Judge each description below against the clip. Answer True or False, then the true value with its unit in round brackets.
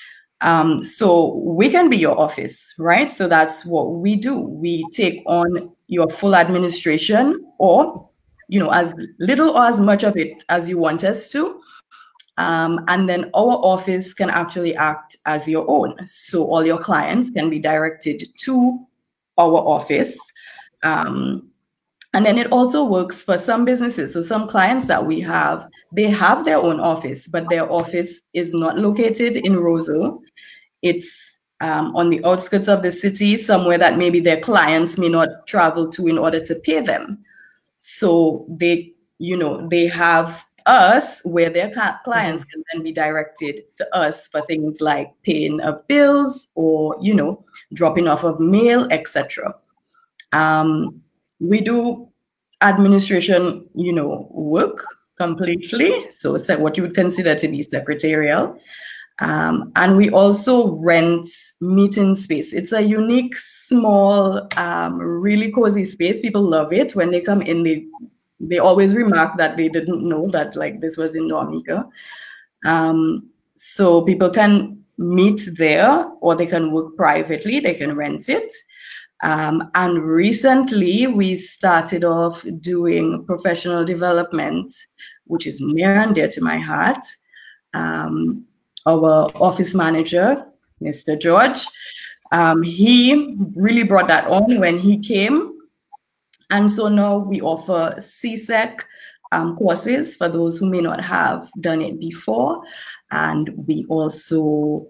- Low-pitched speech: False (175 Hz)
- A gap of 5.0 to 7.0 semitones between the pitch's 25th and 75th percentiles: False (4.3 semitones)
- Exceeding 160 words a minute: False (145 wpm)